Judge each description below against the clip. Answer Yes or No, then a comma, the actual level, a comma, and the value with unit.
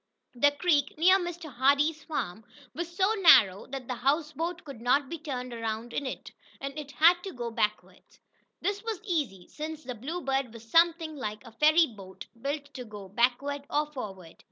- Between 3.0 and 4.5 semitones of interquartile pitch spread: No, average, 5.3 semitones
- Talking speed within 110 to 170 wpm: No, average, 180 wpm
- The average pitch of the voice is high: Yes, very high, 280 Hz